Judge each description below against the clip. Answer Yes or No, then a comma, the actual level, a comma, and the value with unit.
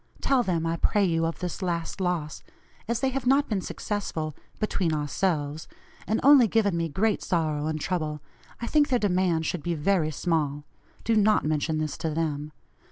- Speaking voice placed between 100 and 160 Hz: No, medium, 170 Hz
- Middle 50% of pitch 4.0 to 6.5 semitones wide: Yes, average, 5.1 semitones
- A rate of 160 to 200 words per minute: Yes, average, 180 wpm